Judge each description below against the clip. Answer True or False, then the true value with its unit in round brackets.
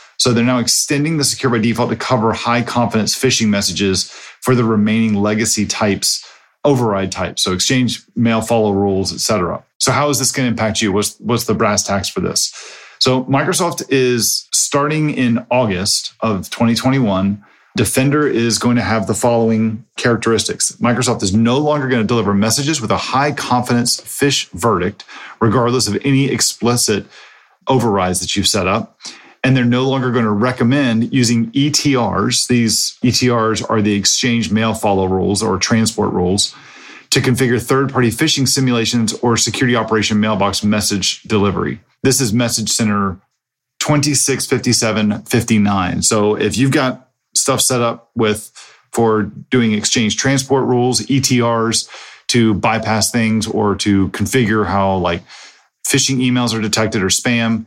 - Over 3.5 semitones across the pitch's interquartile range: False (3.2 semitones)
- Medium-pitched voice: False (115 Hz)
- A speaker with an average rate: True (150 wpm)